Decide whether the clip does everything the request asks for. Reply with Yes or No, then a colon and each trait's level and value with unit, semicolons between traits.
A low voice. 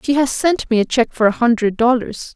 No: high, 240 Hz